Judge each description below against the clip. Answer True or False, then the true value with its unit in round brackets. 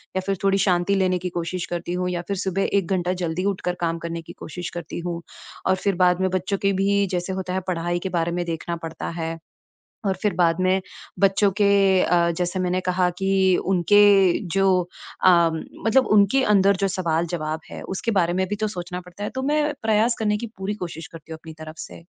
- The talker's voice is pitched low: False (185 Hz)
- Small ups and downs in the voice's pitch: True (2.3 semitones)